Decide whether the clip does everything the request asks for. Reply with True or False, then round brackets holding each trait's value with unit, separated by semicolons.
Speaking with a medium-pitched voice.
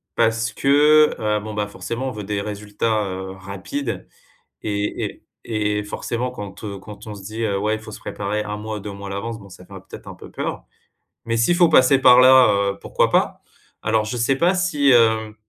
False (110 Hz)